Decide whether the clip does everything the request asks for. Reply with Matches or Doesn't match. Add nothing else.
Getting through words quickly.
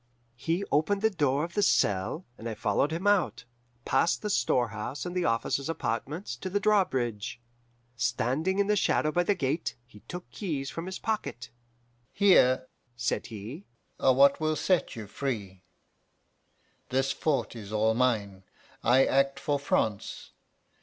Doesn't match